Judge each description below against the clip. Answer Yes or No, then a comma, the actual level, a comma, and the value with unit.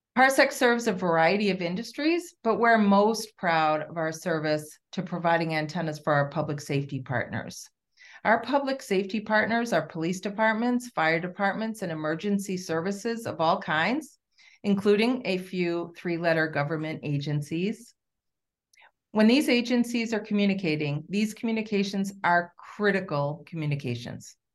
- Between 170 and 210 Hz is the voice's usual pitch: Yes, medium, 185 Hz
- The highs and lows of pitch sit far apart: Yes, wide, 5.7 semitones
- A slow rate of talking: Yes, slow, 130 wpm